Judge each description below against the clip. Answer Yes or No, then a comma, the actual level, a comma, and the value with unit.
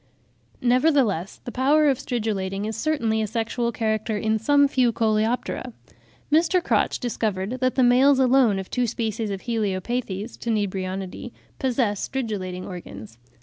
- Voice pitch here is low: No, high, 225 Hz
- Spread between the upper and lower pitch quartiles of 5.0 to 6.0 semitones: No, average, 4.0 semitones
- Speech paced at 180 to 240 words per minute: No, slow, 135 wpm